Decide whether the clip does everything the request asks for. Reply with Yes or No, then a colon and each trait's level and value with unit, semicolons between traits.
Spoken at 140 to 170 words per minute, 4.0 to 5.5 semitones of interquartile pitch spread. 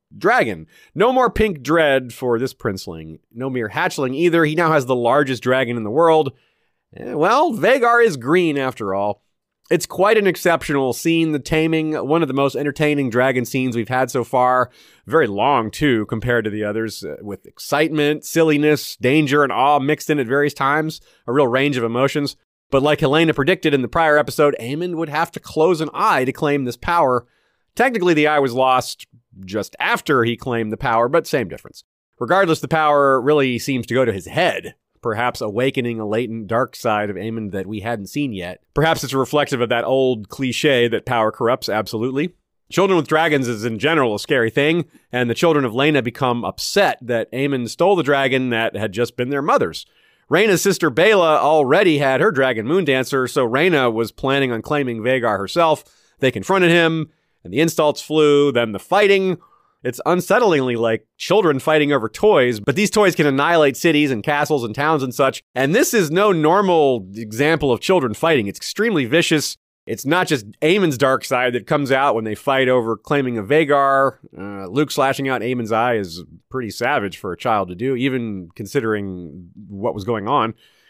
No: average, 190 wpm; average, 4.7 semitones